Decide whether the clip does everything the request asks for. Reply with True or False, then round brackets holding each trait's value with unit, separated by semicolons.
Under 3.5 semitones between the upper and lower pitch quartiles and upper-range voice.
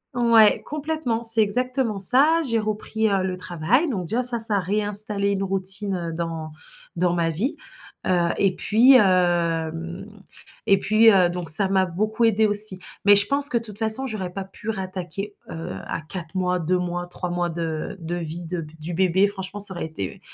False (3.8 semitones; 195 Hz)